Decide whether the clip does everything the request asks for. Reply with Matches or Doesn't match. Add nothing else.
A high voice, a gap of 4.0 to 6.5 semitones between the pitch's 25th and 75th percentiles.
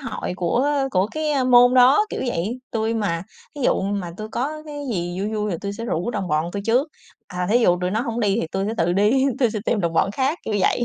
Matches